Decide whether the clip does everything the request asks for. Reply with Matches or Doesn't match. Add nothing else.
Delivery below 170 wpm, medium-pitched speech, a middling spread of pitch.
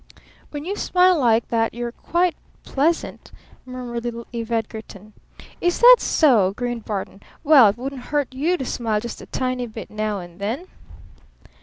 Doesn't match